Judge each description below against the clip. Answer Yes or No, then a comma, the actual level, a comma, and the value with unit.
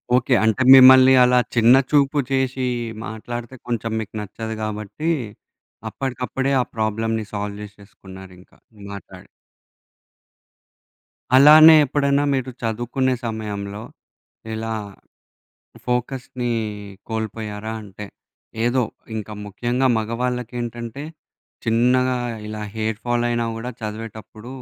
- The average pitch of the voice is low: Yes, low, 115 Hz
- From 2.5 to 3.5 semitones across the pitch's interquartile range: Yes, average, 2.9 semitones